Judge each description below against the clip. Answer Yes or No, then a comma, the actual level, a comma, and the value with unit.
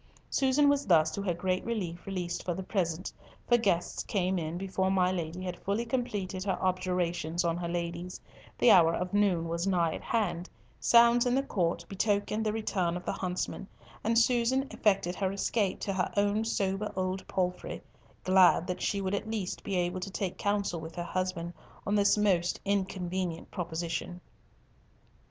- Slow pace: No, average, 175 wpm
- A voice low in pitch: No, medium, 185 Hz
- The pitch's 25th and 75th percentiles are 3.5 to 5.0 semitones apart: No, average, 2.7 semitones